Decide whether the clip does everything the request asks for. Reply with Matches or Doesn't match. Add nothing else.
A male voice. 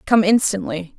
Doesn't match